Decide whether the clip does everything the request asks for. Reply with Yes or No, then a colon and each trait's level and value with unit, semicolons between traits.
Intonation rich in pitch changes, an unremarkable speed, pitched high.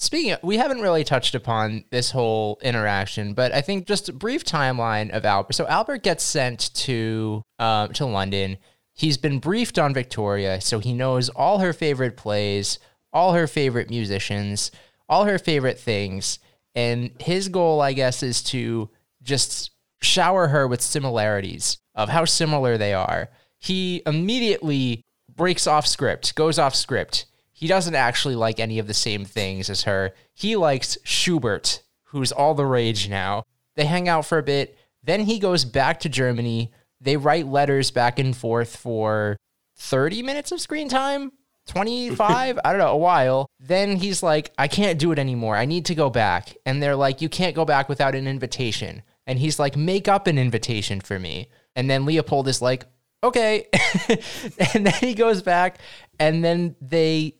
No: wide, 6.8 semitones; average, 175 wpm; low, 135 Hz